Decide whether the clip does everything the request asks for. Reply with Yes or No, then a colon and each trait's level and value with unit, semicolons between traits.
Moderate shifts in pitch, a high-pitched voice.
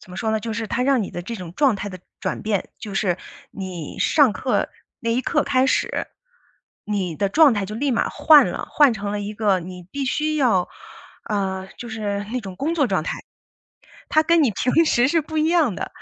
No: wide, 6.1 semitones; high, 220 Hz